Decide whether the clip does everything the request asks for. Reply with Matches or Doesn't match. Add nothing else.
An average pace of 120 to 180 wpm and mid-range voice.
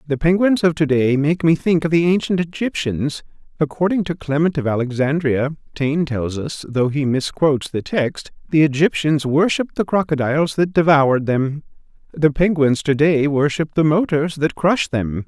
Matches